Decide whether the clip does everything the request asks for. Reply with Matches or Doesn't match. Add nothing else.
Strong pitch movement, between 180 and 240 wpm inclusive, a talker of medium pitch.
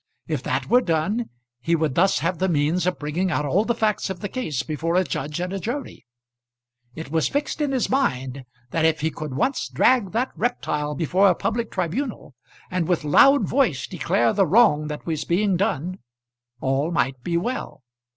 Matches